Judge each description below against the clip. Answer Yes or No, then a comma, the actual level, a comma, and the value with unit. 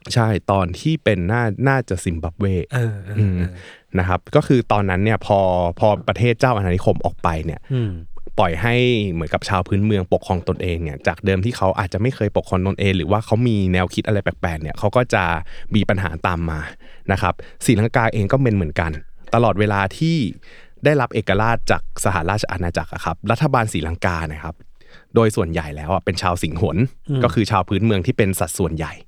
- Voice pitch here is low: Yes, low, 100 Hz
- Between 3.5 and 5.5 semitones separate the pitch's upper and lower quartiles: Yes, average, 4.1 semitones